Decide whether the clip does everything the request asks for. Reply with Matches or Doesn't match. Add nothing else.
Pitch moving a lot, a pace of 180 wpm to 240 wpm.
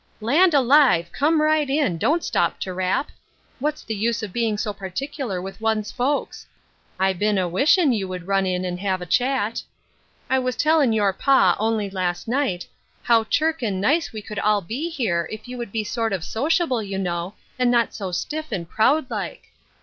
Matches